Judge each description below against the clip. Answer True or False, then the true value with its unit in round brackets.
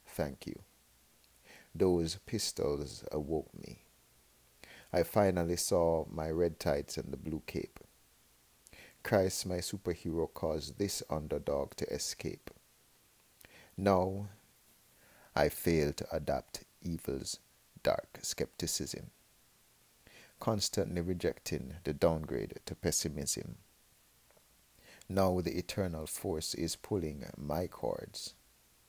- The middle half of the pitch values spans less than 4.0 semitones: True (3.0 semitones)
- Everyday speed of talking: False (95 wpm)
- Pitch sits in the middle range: False (90 Hz)